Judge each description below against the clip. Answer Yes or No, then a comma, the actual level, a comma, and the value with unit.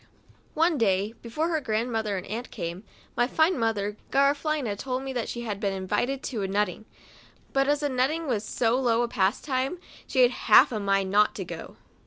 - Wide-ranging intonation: No, average, 4.6 semitones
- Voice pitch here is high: Yes, high, 240 Hz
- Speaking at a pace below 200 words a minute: No, fast, 205 wpm